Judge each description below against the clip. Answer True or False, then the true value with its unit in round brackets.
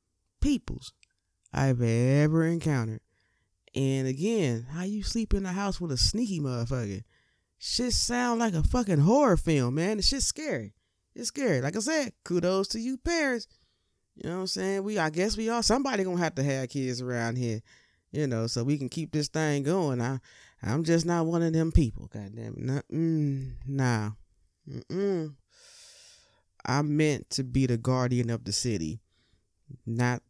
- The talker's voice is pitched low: False (145 Hz)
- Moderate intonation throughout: False (8.2 semitones)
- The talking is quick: False (170 wpm)